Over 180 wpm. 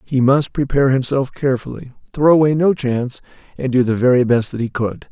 Yes: average, 200 wpm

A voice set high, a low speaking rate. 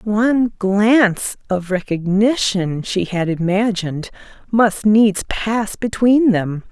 Yes: high, 205 Hz; slow, 105 wpm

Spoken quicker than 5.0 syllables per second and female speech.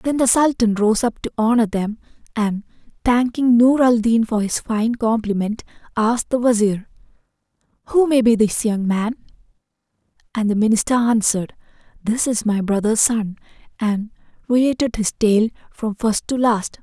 No: 4.8 syllables/s; female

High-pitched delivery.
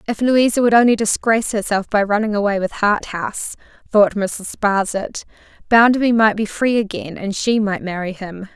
Yes: high, 210 Hz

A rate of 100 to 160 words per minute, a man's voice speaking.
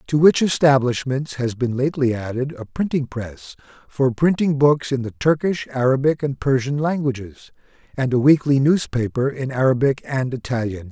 Yes: average, 155 wpm; male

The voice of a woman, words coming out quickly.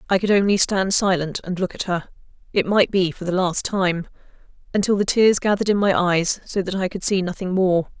Yes: female; fast, 210 wpm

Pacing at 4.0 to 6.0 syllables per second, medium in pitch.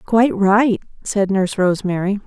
No: 5.4 syllables/s; high, 200 Hz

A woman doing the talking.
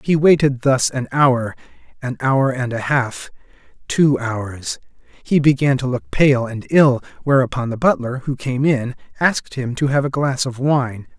No: male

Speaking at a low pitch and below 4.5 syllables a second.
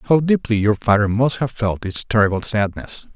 No: low, 110 Hz; 4.9 syllables/s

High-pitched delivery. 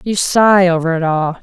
No: medium, 180 Hz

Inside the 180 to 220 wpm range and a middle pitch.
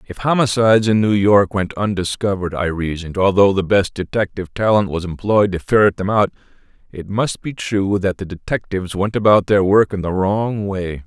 No: average, 190 wpm; low, 100 Hz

